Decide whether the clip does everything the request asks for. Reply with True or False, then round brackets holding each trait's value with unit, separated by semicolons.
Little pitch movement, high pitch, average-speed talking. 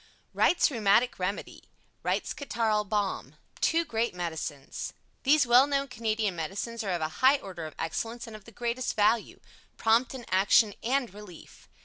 False (4.0 semitones; 220 Hz; 155 wpm)